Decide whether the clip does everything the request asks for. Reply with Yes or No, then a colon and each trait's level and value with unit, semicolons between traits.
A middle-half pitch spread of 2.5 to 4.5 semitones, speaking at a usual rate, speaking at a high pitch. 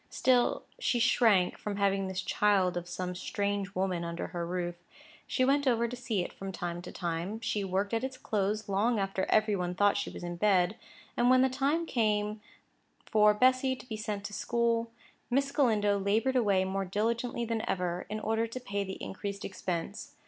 Yes: average, 3.7 semitones; average, 190 wpm; high, 205 Hz